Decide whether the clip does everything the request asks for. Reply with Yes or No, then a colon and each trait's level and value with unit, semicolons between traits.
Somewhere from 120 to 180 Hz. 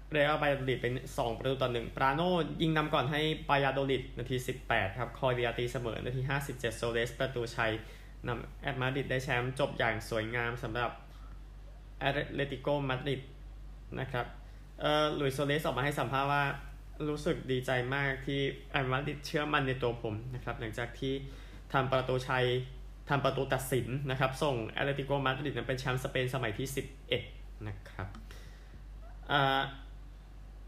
Yes: low, 130 Hz